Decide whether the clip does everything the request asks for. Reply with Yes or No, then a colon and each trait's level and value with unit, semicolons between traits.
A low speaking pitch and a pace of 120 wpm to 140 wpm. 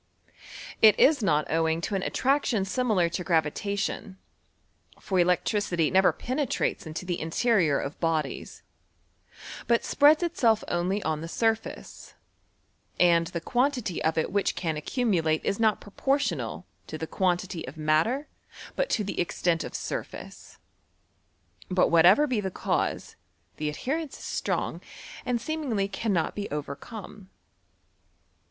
No: high, 190 Hz; slow, 135 wpm